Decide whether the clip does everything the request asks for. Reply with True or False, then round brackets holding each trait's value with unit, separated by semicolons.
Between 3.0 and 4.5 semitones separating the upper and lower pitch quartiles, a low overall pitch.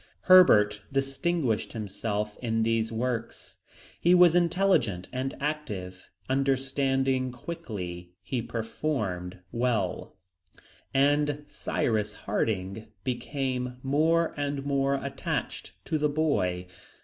False (5.1 semitones; 130 Hz)